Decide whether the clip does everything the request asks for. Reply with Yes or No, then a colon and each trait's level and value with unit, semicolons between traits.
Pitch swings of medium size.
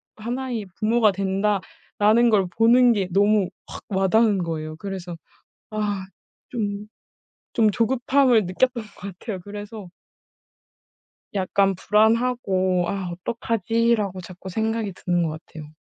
Yes: average, 3.3 semitones